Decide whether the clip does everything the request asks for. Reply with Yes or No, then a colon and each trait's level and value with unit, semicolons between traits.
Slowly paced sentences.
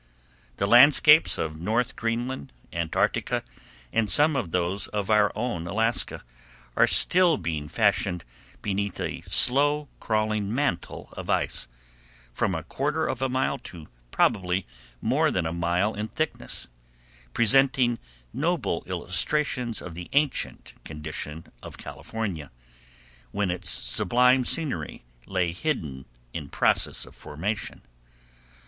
Yes: slow, 120 wpm